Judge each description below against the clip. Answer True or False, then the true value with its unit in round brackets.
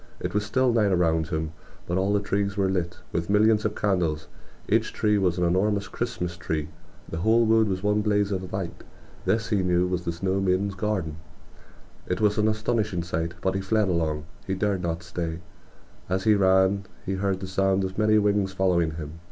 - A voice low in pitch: True (95 Hz)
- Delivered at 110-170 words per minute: False (200 wpm)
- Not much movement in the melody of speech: False (3.0 semitones)